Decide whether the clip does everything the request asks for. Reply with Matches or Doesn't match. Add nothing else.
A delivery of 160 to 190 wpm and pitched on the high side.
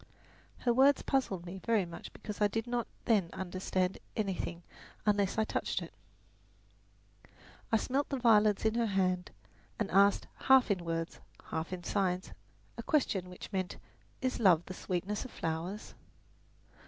Doesn't match